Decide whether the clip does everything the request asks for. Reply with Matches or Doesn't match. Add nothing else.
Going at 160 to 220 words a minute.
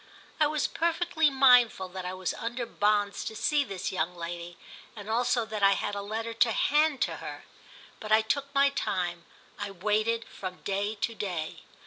Matches